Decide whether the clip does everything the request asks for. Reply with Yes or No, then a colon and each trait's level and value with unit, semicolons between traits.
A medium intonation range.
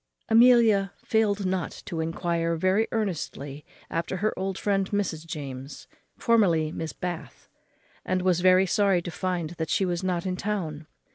Yes: average, 3.2 semitones